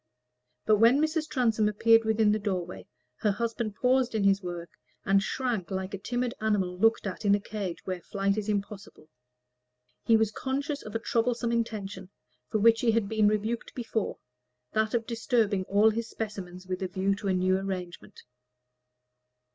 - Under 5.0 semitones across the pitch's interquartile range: Yes, average, 2.9 semitones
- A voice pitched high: Yes, high, 215 Hz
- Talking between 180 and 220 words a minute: No, average, 170 wpm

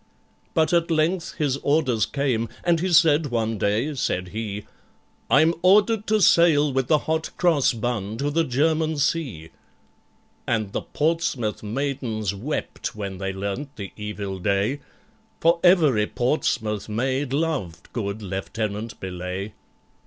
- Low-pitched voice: Yes, low, 125 Hz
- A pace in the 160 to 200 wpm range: No, slow, 135 wpm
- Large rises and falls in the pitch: Yes, wide, 7.0 semitones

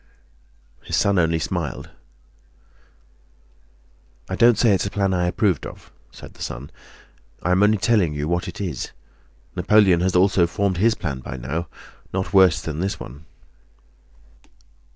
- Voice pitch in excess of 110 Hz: No, very low, 90 Hz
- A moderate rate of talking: Yes, average, 150 wpm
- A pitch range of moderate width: Yes, average, 3.4 semitones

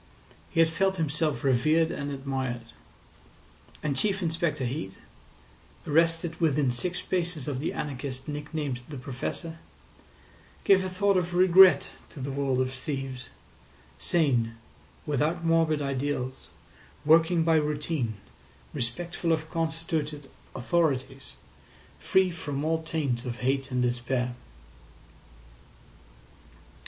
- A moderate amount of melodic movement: Yes, average, 3.8 semitones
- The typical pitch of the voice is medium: Yes, medium, 150 Hz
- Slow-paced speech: Yes, slow, 110 wpm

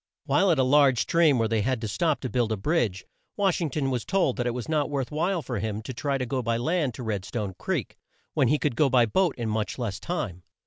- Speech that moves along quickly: Yes, fast, 265 wpm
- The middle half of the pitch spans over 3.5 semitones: Yes, average, 5.1 semitones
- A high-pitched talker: No, low, 130 Hz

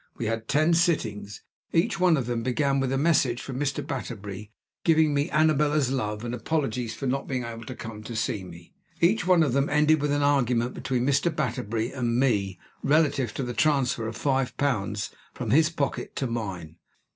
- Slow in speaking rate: No, average, 190 wpm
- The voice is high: No, low, 130 Hz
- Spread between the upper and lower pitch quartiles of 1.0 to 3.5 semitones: No, average, 4.4 semitones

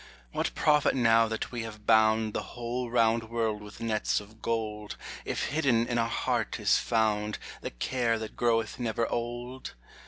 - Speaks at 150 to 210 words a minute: Yes, average, 165 wpm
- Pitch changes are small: Yes, narrow, 1.5 semitones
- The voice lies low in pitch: Yes, low, 115 Hz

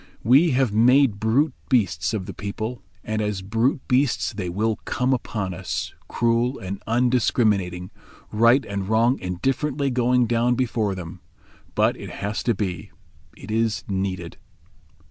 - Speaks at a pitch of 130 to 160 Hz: No, low, 110 Hz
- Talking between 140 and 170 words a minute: Yes, average, 145 wpm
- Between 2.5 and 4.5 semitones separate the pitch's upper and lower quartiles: Yes, average, 4.1 semitones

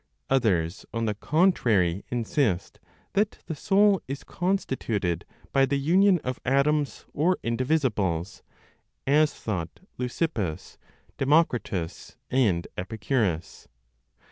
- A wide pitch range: Yes, wide, 7.4 semitones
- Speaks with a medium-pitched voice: No, low, 130 Hz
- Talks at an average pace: No, slow, 95 wpm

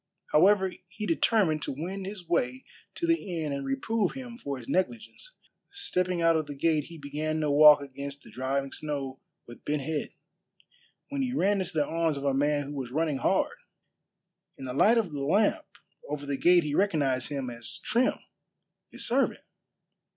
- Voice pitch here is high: No, medium, 155 Hz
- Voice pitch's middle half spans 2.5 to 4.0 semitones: No, wide, 5.4 semitones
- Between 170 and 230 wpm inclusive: Yes, average, 180 wpm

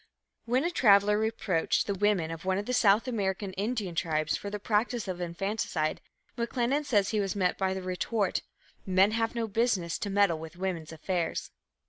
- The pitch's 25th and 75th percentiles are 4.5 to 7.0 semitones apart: No, average, 3.5 semitones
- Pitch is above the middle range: Yes, high, 200 Hz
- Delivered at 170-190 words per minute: Yes, average, 180 wpm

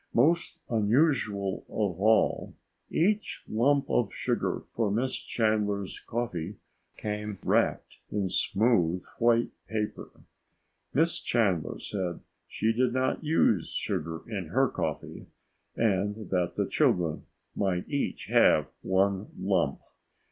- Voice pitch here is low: Yes, low, 105 Hz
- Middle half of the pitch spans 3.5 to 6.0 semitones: Yes, average, 4.0 semitones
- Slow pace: Yes, slow, 110 wpm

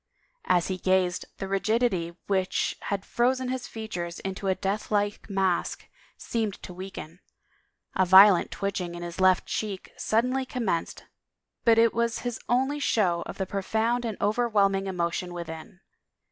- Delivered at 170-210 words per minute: No, average, 145 wpm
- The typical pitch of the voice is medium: No, high, 195 Hz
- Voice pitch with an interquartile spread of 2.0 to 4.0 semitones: Yes, average, 3.7 semitones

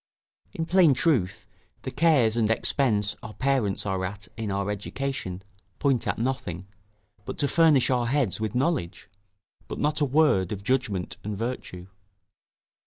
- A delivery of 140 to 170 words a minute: Yes, average, 150 wpm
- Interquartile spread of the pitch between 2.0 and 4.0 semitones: No, wide, 5.6 semitones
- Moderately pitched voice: No, low, 120 Hz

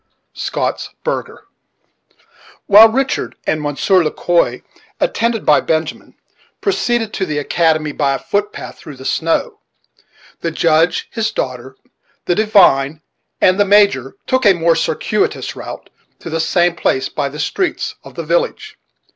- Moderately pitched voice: Yes, medium, 170 Hz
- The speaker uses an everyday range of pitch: No, wide, 5.9 semitones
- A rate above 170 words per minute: No, average, 145 wpm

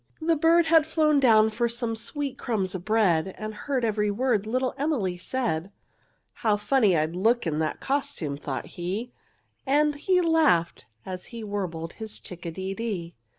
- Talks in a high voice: Yes, high, 220 Hz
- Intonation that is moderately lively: No, wide, 6.9 semitones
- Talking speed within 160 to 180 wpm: Yes, average, 170 wpm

